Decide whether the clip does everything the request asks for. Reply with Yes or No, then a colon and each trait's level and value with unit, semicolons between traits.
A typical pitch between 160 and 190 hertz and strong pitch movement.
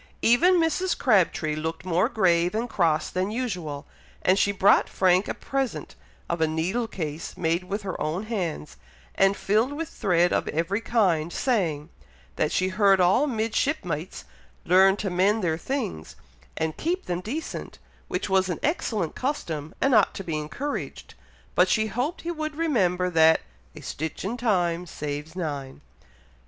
Yes: medium, 185 Hz; wide, 5.8 semitones